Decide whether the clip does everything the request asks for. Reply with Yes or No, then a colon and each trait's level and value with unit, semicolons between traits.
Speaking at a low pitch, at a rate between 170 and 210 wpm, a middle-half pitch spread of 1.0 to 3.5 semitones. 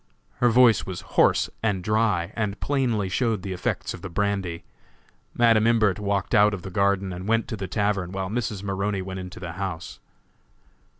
Yes: low, 100 Hz; average, 180 wpm; average, 2.7 semitones